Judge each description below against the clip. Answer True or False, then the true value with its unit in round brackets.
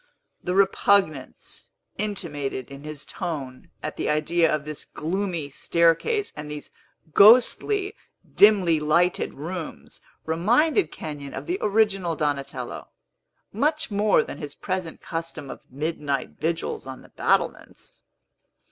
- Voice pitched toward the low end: False (165 Hz)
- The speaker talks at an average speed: False (120 wpm)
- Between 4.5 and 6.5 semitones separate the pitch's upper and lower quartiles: True (5.2 semitones)